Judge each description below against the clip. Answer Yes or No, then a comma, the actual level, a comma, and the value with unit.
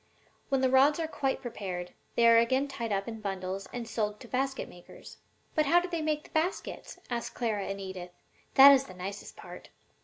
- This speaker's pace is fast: Yes, fast, 210 wpm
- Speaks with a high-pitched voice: Yes, high, 235 Hz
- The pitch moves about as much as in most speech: No, wide, 5.8 semitones